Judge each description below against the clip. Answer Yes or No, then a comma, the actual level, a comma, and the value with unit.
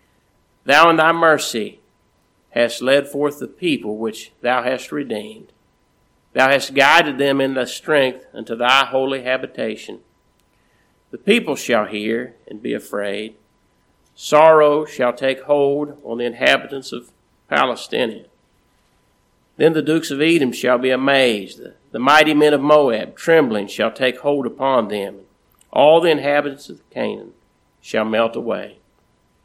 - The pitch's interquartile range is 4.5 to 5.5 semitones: No, average, 3.8 semitones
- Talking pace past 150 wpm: No, average, 140 wpm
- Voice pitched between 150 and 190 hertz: No, low, 135 Hz